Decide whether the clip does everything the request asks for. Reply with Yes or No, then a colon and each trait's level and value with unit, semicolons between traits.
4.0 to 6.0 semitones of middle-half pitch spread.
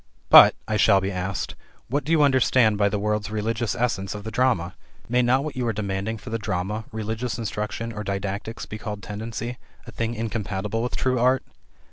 No: average, 2.8 semitones